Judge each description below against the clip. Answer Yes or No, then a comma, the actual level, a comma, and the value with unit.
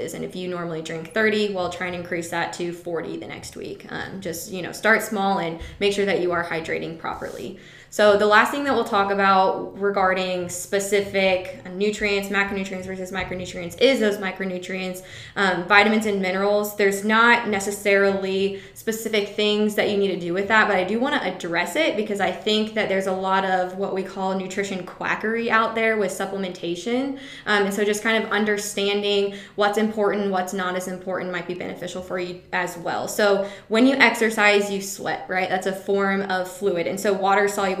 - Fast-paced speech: No, average, 195 wpm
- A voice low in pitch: No, high, 195 Hz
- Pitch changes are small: Yes, narrow, 2.1 semitones